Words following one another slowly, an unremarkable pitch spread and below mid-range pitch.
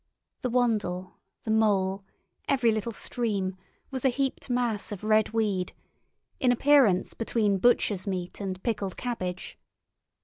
No: slow, 130 wpm; average, 4.2 semitones; high, 215 Hz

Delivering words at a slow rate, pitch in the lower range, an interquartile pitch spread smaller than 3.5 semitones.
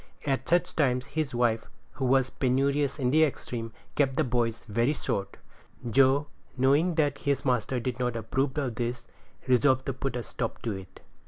No: average, 175 wpm; low, 130 Hz; average, 2.7 semitones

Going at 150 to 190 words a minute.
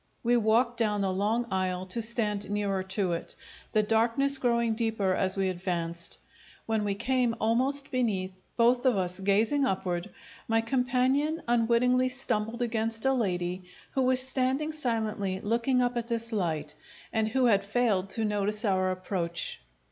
Yes: average, 155 wpm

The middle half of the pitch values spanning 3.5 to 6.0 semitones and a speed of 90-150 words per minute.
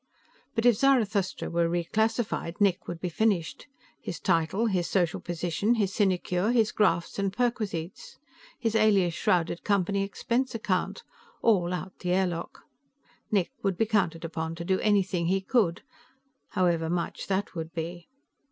Yes: average, 3.9 semitones; average, 145 wpm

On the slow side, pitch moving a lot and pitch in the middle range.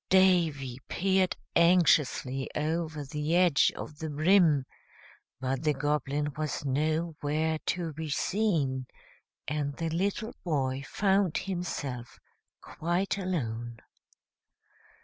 No: slow, 100 wpm; average, 3.9 semitones; medium, 155 Hz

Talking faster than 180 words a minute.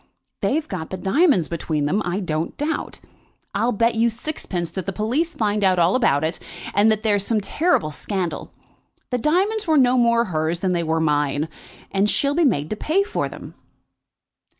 Yes: average, 190 wpm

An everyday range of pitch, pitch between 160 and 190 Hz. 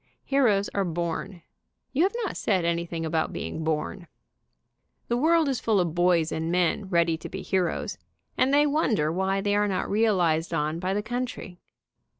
Yes: average, 4.6 semitones; medium, 185 Hz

